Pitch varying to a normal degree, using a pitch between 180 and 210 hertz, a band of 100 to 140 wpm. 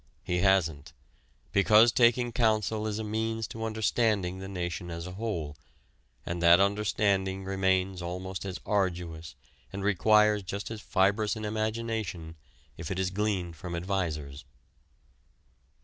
No: average, 3.5 semitones; very low, 95 Hz; slow, 135 wpm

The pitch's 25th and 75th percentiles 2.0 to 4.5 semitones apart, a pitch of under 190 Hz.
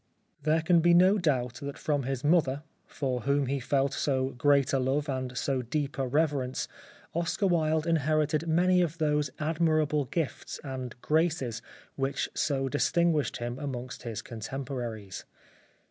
Yes: average, 3.3 semitones; medium, 140 Hz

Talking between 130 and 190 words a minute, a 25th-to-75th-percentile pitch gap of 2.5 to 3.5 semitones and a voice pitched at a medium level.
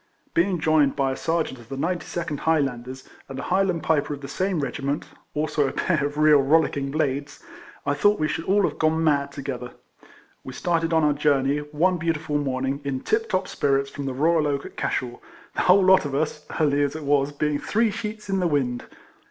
No: fast, 205 wpm; average, 3.0 semitones; medium, 150 Hz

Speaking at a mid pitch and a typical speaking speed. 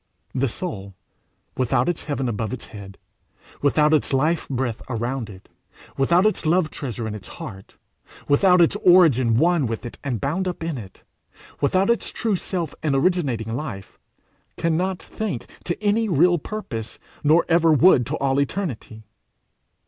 Yes: medium, 145 Hz; average, 155 wpm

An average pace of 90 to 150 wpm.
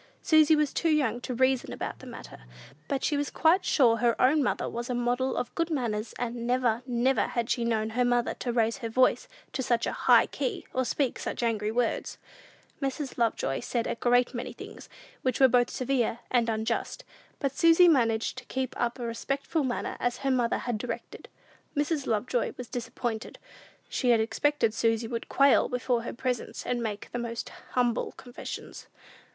No: average, 185 wpm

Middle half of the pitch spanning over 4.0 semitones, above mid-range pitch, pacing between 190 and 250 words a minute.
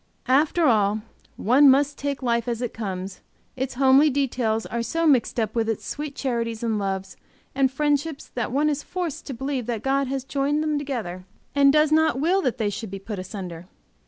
Yes: average, 4.4 semitones; very high, 260 Hz; average, 195 wpm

